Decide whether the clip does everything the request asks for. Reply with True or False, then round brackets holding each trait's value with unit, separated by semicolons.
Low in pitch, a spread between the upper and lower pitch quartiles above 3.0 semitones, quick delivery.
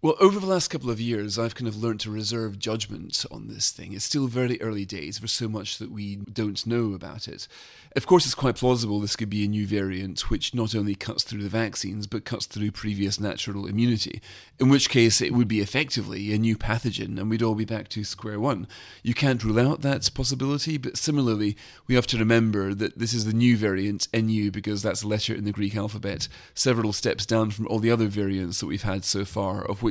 False (110 Hz; 2.6 semitones; 235 wpm)